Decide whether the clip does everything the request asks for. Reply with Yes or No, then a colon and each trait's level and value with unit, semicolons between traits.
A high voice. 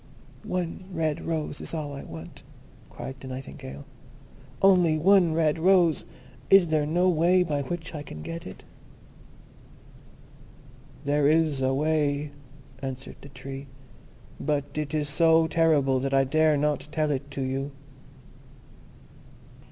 No: medium, 150 Hz